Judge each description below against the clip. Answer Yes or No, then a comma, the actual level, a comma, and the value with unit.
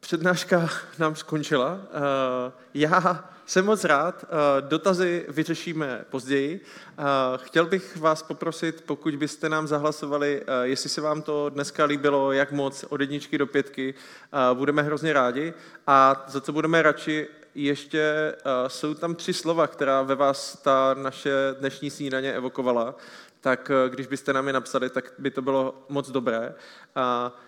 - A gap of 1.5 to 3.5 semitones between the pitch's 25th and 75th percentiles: Yes, narrow, 2.6 semitones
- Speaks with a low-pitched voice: No, medium, 145 Hz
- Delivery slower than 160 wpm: Yes, average, 140 wpm